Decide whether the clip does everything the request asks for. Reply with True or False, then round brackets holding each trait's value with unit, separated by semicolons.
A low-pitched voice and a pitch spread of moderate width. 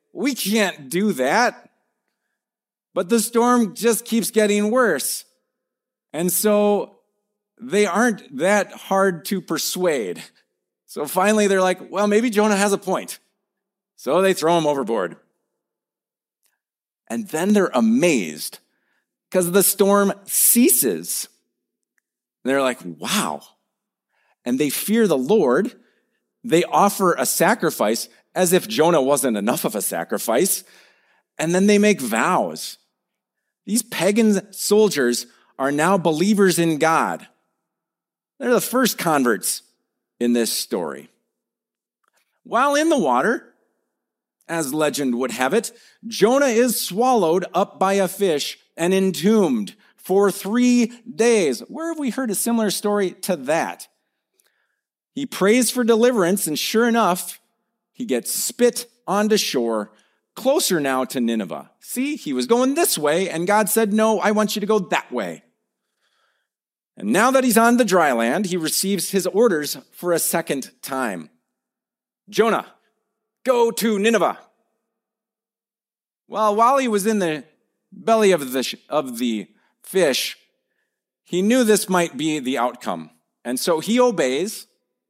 False (205 Hz; 4.6 semitones)